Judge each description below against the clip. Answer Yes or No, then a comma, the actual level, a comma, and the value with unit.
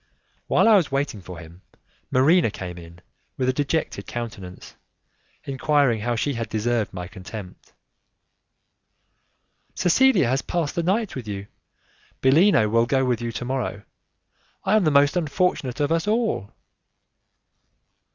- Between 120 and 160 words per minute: Yes, average, 140 wpm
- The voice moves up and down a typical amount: No, wide, 6.8 semitones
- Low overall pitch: Yes, low, 130 Hz